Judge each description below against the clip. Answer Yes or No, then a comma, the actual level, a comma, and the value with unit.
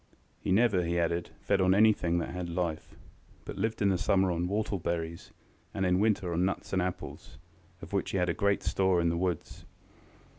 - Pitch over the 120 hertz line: No, very low, 90 Hz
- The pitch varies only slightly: Yes, narrow, 2.3 semitones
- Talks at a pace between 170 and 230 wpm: Yes, average, 195 wpm